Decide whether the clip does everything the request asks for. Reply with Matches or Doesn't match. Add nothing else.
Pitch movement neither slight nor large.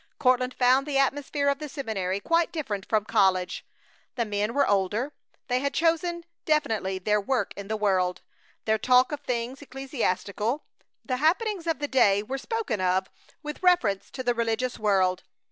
Doesn't match